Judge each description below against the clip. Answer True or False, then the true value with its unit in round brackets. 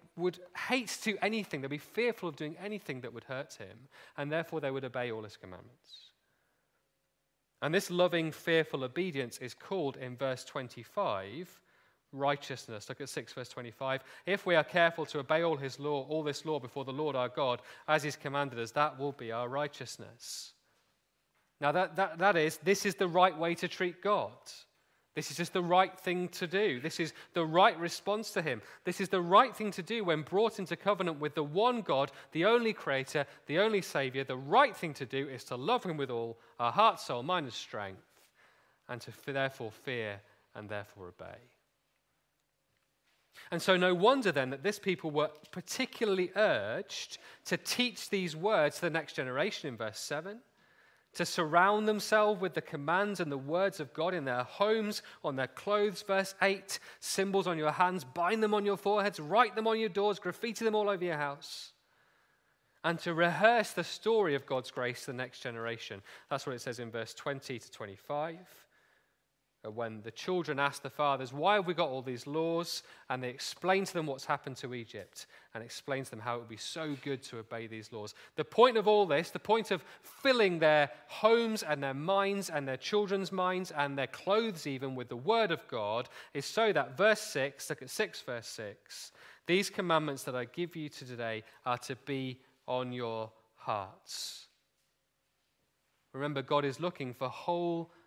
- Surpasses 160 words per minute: True (190 wpm)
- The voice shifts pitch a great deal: True (6.2 semitones)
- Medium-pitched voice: True (155 Hz)